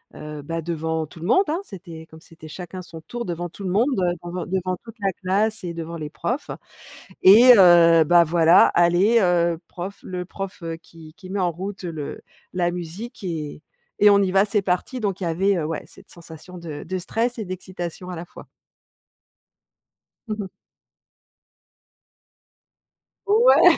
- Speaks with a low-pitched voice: No, medium, 180 Hz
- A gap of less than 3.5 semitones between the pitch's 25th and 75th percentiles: Yes, average, 2.9 semitones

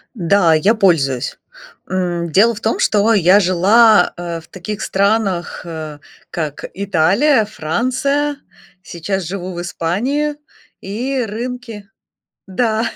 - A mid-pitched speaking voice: No, high, 200 Hz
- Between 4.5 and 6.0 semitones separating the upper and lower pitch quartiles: Yes, average, 4.8 semitones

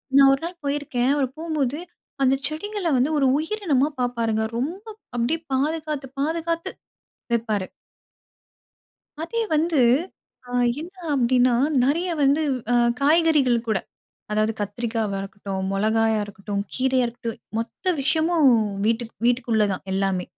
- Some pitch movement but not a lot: No, wide, 5.9 semitones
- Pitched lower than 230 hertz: No, very high, 260 Hz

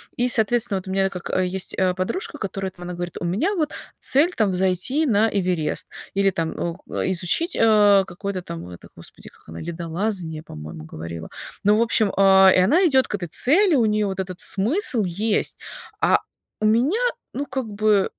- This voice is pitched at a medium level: No, high, 195 Hz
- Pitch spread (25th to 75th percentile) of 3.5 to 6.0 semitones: Yes, average, 4.1 semitones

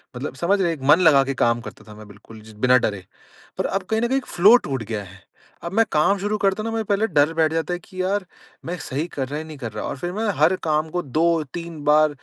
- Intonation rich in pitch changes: Yes, wide, 6.0 semitones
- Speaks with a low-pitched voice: No, medium, 155 Hz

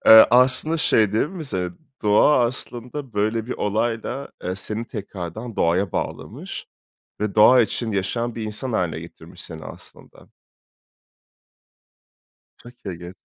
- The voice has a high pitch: No, low, 110 Hz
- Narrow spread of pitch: No, average, 3.9 semitones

